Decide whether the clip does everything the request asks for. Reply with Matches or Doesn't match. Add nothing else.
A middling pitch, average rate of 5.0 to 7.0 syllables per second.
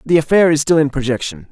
Matches